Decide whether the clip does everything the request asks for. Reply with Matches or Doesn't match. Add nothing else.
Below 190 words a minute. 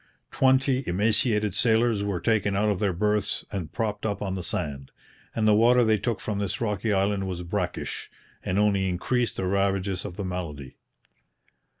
Matches